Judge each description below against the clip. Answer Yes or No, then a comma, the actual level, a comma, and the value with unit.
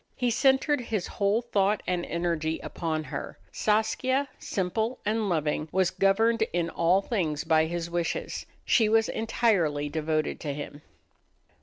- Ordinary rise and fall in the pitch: No, wide, 5.7 semitones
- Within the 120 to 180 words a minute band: Yes, average, 140 wpm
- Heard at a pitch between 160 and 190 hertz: Yes, medium, 185 Hz